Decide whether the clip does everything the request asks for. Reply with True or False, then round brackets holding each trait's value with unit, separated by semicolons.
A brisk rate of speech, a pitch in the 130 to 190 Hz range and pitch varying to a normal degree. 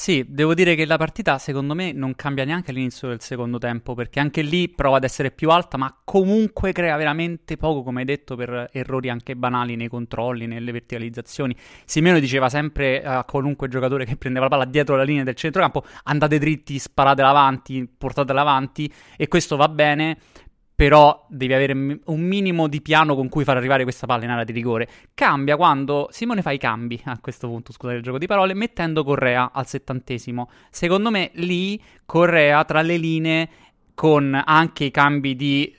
True (185 wpm; 140 Hz; 3.5 semitones)